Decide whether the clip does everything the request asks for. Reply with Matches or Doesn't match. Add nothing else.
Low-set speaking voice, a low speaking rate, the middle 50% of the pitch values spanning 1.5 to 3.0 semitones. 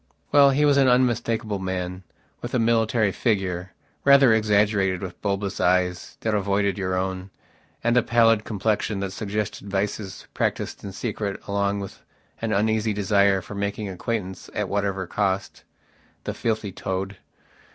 Doesn't match